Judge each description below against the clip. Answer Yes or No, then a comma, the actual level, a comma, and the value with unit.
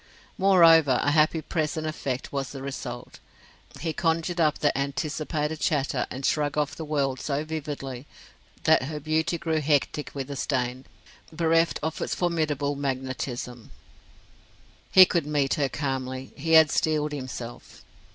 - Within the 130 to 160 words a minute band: Yes, average, 140 wpm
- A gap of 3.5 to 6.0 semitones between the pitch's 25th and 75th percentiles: No, average, 2.9 semitones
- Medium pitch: Yes, medium, 150 Hz